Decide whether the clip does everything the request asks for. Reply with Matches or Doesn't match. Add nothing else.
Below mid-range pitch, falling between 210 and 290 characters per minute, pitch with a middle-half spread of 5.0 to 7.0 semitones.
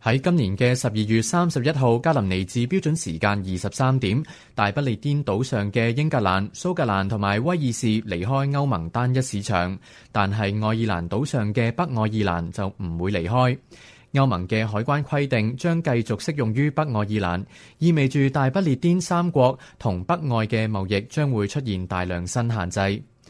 Matches